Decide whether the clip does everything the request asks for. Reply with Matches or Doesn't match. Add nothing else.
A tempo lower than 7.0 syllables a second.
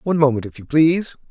Doesn't match